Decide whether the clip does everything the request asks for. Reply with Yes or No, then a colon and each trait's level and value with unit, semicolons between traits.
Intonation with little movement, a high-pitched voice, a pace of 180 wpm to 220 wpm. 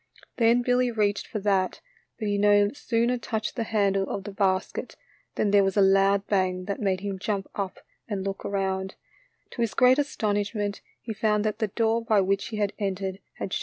Yes: narrow, 2.2 semitones; high, 205 Hz; average, 200 wpm